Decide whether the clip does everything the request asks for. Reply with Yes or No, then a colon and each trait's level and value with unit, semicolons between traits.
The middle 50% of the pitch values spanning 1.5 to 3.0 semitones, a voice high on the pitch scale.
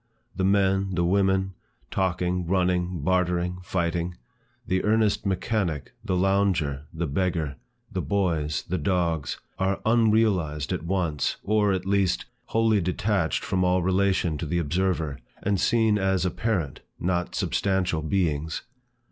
No: narrow, 2.5 semitones; very low, 90 Hz